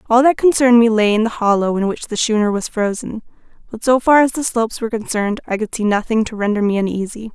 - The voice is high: Yes, high, 225 Hz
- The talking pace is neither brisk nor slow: No, fast, 245 wpm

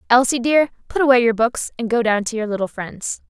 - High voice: Yes, high, 235 Hz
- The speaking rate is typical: No, fast, 235 wpm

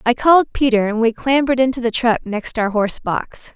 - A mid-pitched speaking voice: No, high, 240 Hz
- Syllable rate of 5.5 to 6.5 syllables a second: Yes, 5.7 syllables/s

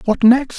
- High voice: Yes, high, 245 Hz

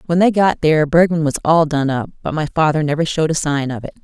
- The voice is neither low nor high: Yes, medium, 155 Hz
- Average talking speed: No, fast, 270 wpm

